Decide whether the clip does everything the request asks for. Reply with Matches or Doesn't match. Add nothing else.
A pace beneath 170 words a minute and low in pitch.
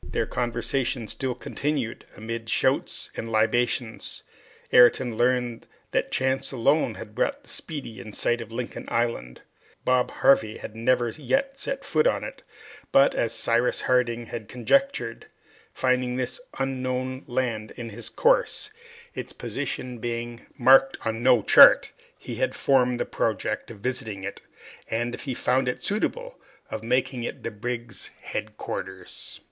Matches